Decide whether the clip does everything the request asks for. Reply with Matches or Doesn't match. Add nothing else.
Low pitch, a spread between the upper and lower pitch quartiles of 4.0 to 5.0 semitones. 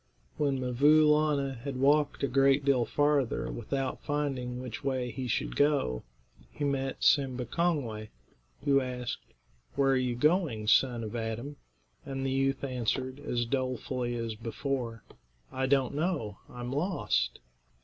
Doesn't match